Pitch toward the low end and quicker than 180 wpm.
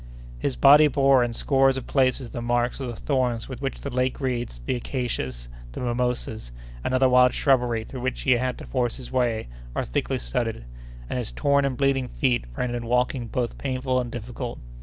Yes: low, 125 Hz; average, 195 wpm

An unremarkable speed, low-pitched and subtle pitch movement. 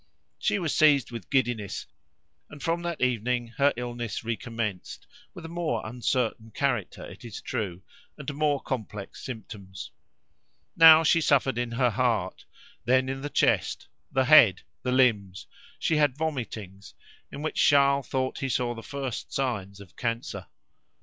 No: average, 150 wpm; low, 125 Hz; average, 3.9 semitones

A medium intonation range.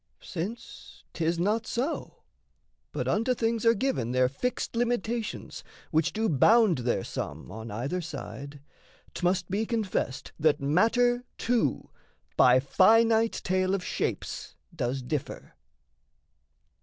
No: wide, 8.3 semitones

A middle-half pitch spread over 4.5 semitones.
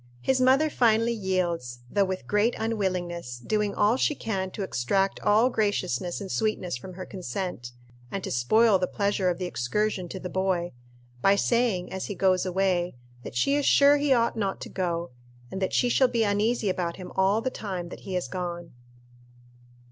No: average, 3.6 semitones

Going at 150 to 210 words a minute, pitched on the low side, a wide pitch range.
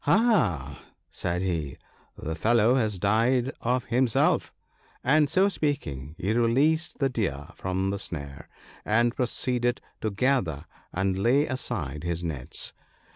No: average, 140 wpm; low, 110 Hz; wide, 7.0 semitones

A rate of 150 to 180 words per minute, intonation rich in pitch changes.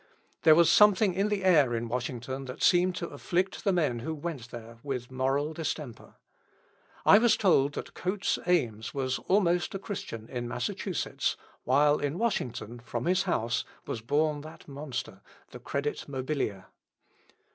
Yes: average, 155 wpm; wide, 6.2 semitones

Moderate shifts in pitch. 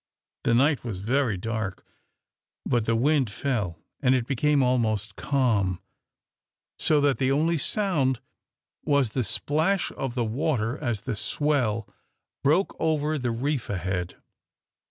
Yes: average, 4.7 semitones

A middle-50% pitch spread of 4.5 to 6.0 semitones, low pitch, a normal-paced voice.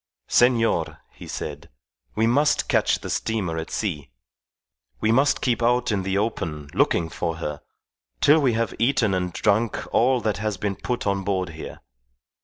Yes: average, 5.1 semitones; low, 105 Hz; average, 165 wpm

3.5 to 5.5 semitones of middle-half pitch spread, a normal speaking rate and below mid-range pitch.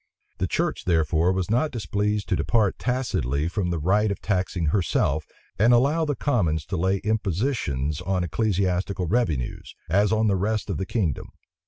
Yes: average, 4.4 semitones; average, 165 wpm; very low, 95 Hz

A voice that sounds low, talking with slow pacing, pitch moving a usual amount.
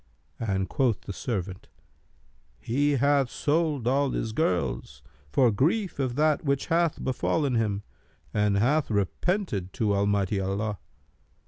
No: low, 120 Hz; slow, 125 wpm; wide, 6.2 semitones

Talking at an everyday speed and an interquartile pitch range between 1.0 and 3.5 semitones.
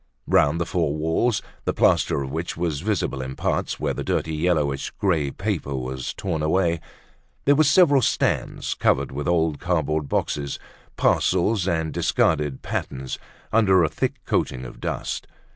No: average, 155 wpm; average, 4.3 semitones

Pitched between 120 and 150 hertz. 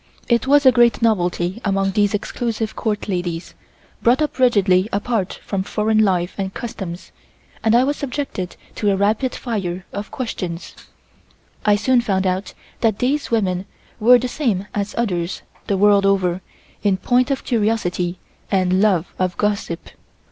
No: high, 205 Hz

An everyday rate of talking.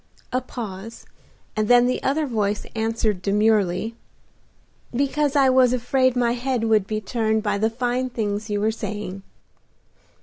Yes: average, 145 wpm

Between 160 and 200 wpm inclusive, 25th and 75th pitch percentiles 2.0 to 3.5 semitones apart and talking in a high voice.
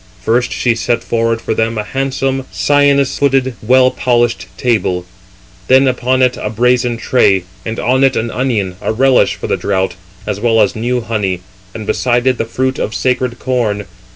No: average, 180 wpm; average, 2.7 semitones; low, 120 Hz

